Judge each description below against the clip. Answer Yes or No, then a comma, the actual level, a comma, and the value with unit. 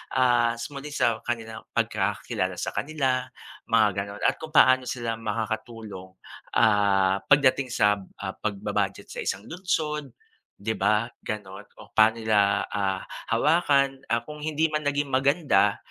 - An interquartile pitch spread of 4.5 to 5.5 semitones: Yes, average, 5.2 semitones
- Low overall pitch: Yes, low, 115 Hz